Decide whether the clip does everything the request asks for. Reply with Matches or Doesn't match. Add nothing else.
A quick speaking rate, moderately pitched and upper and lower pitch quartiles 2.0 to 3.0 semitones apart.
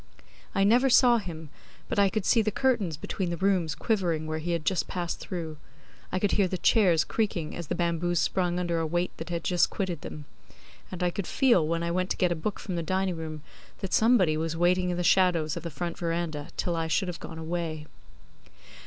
Matches